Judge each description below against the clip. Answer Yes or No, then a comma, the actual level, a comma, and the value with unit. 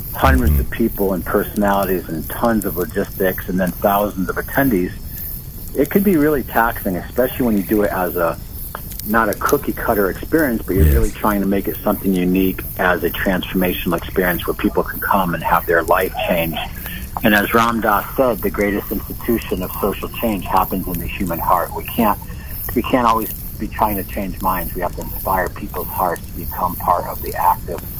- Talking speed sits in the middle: Yes, average, 195 wpm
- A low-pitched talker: Yes, very low, 95 Hz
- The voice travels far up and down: No, average, 2.7 semitones